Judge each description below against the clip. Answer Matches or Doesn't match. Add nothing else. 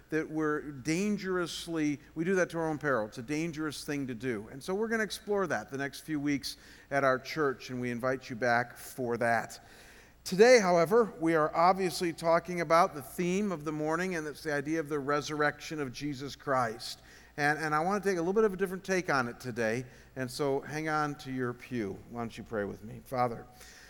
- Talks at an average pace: Doesn't match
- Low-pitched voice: Doesn't match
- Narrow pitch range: Doesn't match